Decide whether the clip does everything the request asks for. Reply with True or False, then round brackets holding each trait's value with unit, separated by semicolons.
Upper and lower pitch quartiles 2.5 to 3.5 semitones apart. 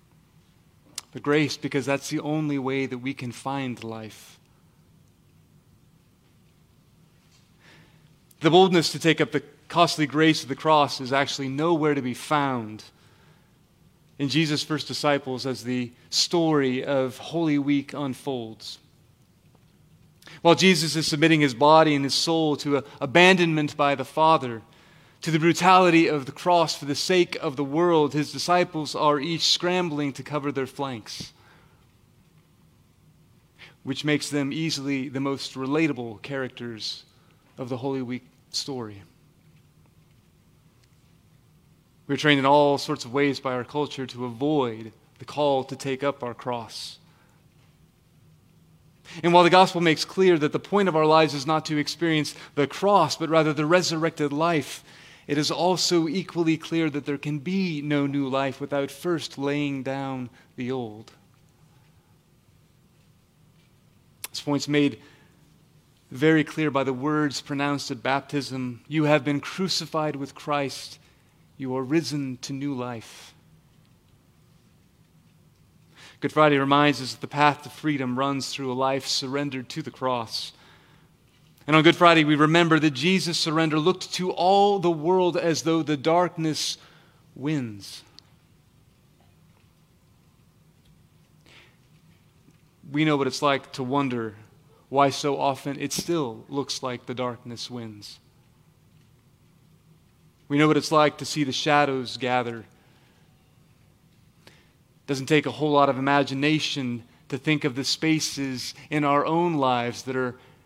True (2.8 semitones)